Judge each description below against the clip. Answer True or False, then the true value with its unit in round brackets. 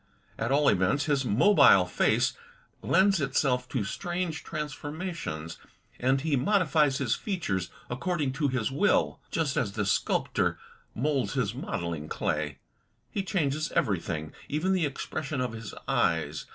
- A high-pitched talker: False (140 Hz)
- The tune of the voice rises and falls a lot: True (6.1 semitones)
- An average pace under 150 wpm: True (140 wpm)